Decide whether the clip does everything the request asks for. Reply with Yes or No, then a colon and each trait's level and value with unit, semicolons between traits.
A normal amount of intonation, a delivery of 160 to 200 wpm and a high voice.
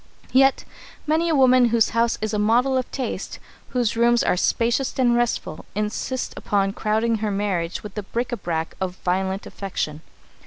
Yes: average, 3.9 semitones; average, 170 wpm; high, 225 Hz